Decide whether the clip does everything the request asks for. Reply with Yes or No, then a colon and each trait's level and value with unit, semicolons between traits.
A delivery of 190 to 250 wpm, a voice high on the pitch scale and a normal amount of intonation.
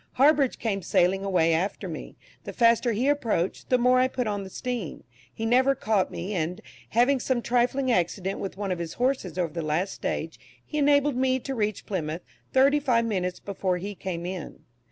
No: average, 195 wpm; high, 215 Hz; wide, 5.8 semitones